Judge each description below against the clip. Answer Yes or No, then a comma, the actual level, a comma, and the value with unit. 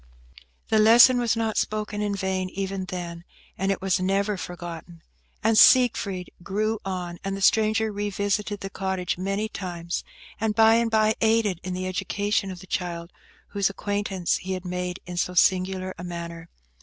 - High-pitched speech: Yes, high, 195 Hz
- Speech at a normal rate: Yes, average, 170 wpm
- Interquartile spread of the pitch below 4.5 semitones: Yes, narrow, 2.6 semitones